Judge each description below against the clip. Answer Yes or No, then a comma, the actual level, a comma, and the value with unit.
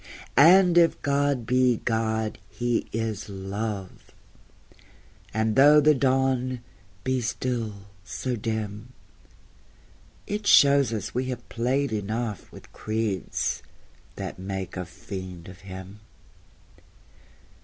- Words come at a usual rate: No, slow, 105 wpm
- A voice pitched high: No, low, 115 Hz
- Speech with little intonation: No, average, 4.2 semitones